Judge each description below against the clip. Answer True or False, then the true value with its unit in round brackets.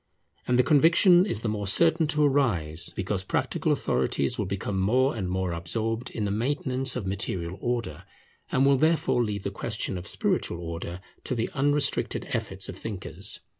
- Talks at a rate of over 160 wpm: True (170 wpm)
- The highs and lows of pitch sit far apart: True (6.1 semitones)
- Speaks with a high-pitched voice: False (110 Hz)